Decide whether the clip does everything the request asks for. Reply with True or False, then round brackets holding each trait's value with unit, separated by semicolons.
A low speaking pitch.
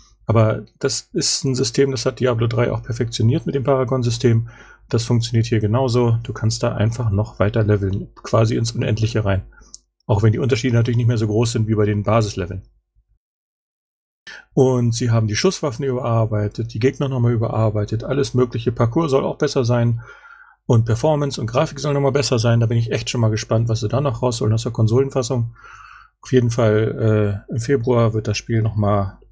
True (120 Hz)